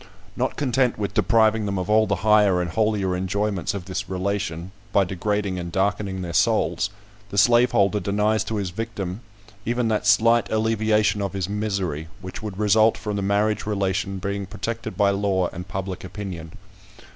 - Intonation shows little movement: Yes, narrow, 2.3 semitones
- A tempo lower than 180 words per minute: Yes, average, 170 wpm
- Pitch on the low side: Yes, low, 100 Hz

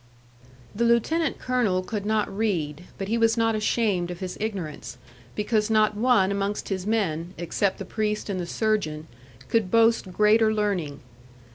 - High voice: Yes, high, 210 Hz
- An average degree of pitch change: Yes, average, 3.4 semitones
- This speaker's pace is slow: No, average, 155 wpm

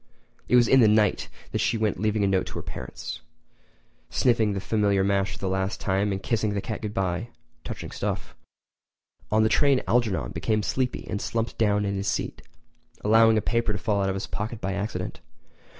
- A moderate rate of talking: Yes, average, 195 wpm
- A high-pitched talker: No, low, 105 Hz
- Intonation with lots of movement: No, narrow, 2.4 semitones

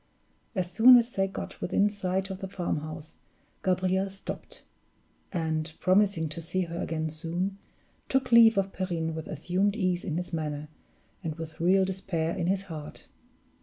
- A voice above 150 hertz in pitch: Yes, medium, 185 Hz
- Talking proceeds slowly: No, average, 160 wpm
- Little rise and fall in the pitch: No, average, 3.1 semitones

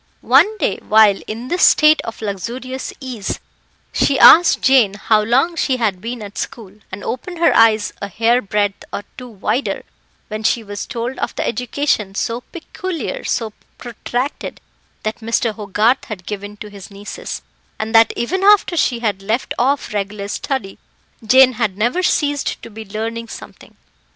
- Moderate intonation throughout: Yes, average, 3.9 semitones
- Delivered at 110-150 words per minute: No, average, 165 wpm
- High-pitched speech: Yes, high, 230 Hz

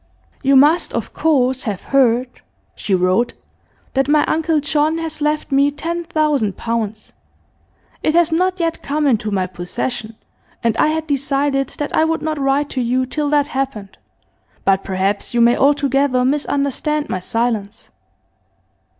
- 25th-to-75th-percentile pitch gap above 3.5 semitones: Yes, average, 4.5 semitones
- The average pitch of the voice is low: No, very high, 275 Hz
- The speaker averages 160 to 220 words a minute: No, average, 150 wpm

